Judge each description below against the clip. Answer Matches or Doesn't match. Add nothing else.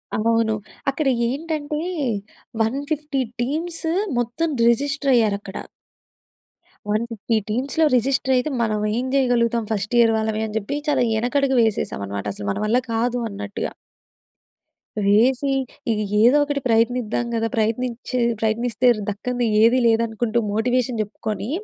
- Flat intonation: Doesn't match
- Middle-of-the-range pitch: Doesn't match